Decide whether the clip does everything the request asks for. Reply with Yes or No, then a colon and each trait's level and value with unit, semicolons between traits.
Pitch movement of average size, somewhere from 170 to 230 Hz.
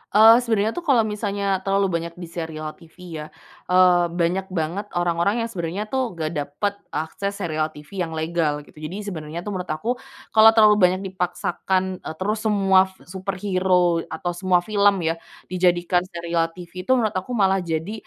Yes: average, 3.0 semitones; medium, 185 Hz